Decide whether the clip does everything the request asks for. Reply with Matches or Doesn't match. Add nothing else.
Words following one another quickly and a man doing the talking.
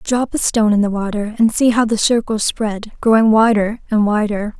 Doesn't match